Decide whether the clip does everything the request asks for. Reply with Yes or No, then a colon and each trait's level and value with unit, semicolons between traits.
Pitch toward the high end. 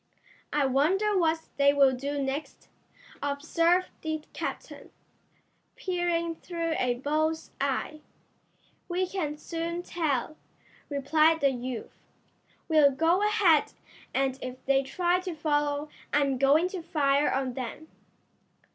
Yes: very high, 305 Hz